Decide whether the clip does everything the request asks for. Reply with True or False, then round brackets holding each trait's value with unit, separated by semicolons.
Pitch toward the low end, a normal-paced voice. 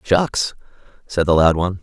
True (90 Hz; 165 wpm)